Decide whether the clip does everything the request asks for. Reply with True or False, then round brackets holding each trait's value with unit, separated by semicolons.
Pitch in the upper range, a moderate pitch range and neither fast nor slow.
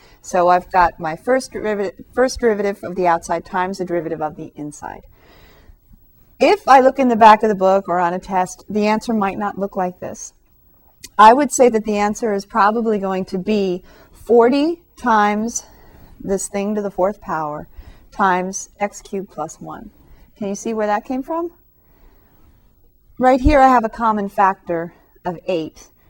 True (200 Hz; 3.6 semitones; 175 wpm)